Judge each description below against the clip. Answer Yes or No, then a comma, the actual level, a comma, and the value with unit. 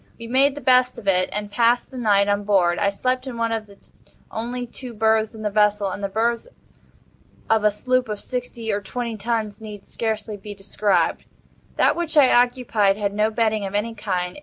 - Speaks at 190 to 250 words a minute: Yes, average, 200 wpm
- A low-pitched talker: No, high, 220 Hz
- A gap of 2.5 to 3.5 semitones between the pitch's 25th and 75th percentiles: Yes, average, 2.8 semitones